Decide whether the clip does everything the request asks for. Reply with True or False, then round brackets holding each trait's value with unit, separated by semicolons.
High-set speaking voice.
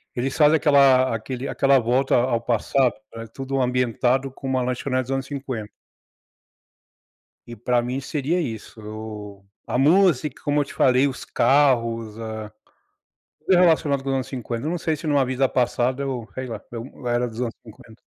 False (130 Hz)